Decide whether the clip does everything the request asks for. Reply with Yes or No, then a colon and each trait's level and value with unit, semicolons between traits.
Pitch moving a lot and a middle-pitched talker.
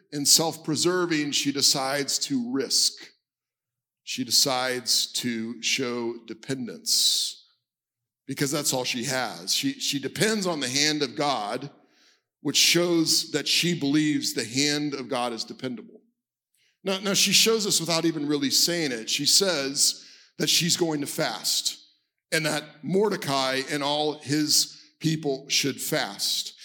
No: average, 3.8 semitones; medium, 150 Hz